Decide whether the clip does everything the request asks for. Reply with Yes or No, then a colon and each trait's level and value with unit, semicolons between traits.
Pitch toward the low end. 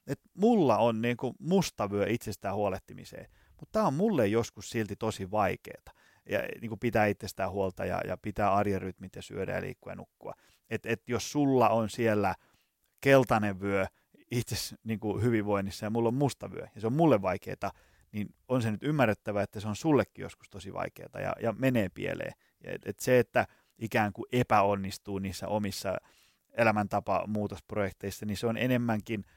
Yes: low, 110 Hz